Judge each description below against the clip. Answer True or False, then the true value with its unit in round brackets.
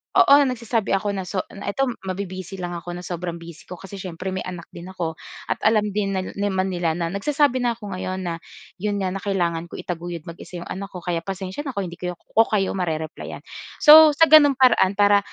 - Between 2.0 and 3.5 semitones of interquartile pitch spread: True (2.7 semitones)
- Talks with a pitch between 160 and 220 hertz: True (190 Hz)